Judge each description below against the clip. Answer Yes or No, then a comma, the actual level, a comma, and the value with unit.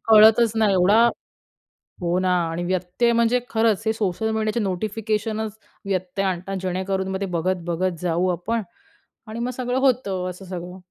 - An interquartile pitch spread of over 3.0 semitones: Yes, average, 3.4 semitones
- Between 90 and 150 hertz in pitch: No, high, 195 Hz